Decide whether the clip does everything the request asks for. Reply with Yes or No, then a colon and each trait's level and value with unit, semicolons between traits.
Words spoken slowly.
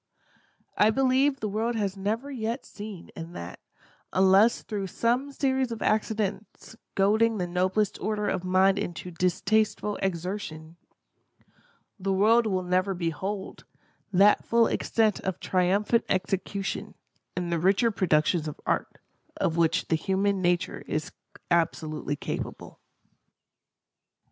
Yes: slow, 125 wpm